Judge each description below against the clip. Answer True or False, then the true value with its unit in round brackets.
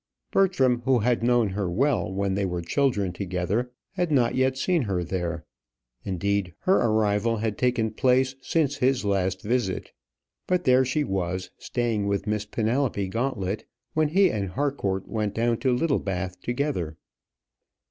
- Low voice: True (110 Hz)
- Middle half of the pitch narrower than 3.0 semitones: False (5.2 semitones)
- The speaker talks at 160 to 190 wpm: False (150 wpm)